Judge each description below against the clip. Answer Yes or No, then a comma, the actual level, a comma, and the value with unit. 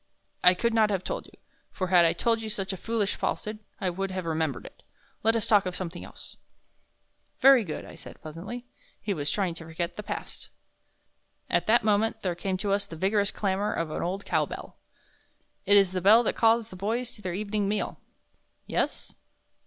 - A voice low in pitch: No, high, 200 Hz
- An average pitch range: Yes, average, 3.2 semitones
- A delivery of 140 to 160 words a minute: No, average, 200 wpm